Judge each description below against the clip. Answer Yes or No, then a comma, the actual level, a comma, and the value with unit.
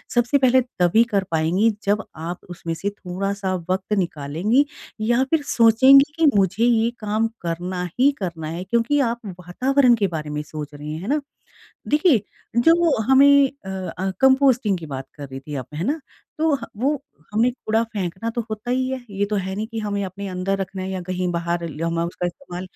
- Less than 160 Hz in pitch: No, high, 200 Hz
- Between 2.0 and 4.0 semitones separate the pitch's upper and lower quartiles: No, wide, 5.5 semitones